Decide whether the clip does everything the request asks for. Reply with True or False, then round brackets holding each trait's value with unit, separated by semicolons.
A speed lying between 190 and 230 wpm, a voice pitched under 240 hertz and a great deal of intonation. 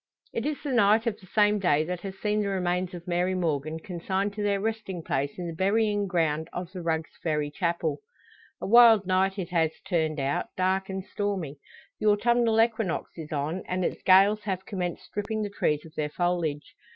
False (200 wpm; 185 Hz; 3.8 semitones)